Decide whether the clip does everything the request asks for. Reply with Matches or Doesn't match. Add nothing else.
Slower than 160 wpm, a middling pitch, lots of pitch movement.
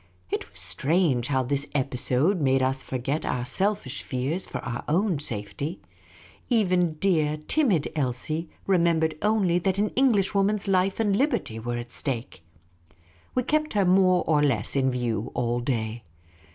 Matches